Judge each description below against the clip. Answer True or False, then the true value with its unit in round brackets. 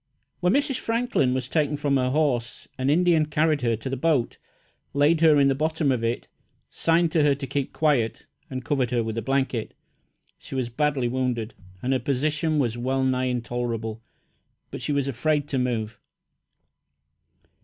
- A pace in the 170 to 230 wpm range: True (175 wpm)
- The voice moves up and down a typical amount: True (3.7 semitones)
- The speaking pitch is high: False (135 Hz)